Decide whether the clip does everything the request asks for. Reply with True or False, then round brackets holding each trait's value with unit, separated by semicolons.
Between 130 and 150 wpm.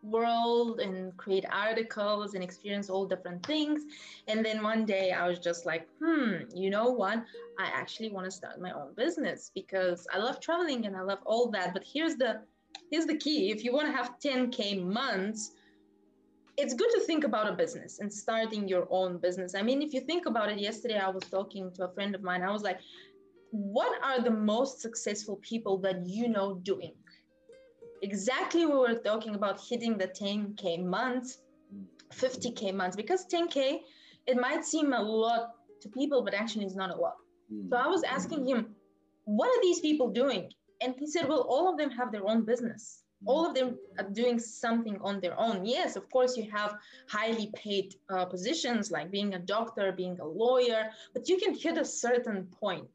False (195 wpm)